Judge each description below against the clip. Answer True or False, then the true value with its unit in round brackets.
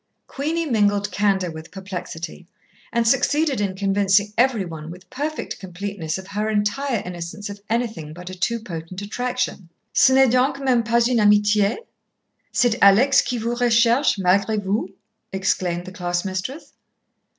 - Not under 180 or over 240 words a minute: False (150 wpm)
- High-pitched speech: True (205 Hz)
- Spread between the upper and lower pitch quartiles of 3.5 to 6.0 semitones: True (4.5 semitones)